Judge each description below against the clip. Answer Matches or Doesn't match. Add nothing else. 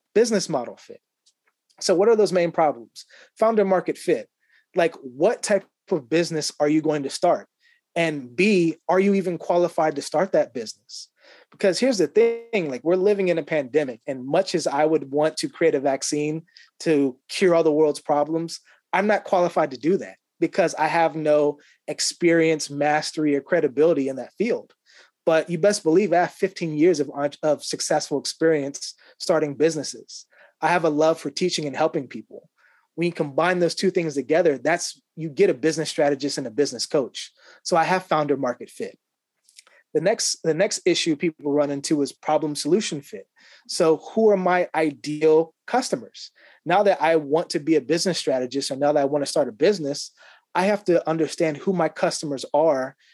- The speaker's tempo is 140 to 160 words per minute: Doesn't match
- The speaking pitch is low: Doesn't match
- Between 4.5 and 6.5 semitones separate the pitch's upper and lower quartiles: Doesn't match